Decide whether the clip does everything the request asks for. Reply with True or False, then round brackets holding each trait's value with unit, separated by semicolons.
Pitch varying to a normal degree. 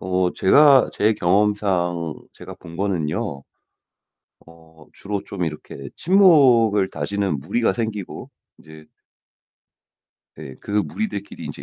True (4.4 semitones)